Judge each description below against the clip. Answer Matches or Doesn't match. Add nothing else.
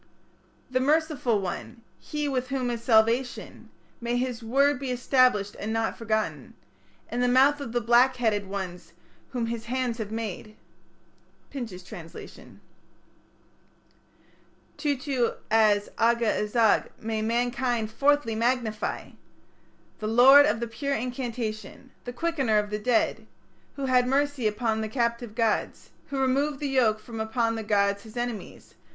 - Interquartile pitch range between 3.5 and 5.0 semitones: Doesn't match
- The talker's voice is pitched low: Doesn't match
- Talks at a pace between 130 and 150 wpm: Matches